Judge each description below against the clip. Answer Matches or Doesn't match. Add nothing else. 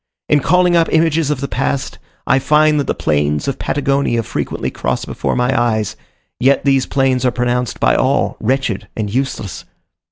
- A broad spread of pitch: Doesn't match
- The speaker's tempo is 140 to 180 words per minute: Matches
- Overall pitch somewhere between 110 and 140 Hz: Matches